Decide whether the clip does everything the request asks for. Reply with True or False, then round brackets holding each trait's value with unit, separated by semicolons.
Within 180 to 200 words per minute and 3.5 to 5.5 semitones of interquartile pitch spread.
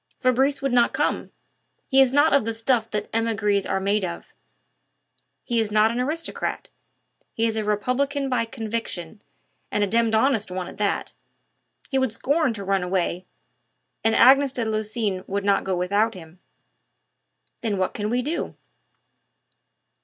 False (160 wpm; 4.0 semitones)